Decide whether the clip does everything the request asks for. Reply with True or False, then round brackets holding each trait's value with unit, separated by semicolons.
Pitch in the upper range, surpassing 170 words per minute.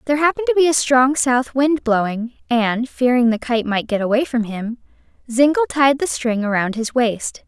True (250 Hz; 200 wpm)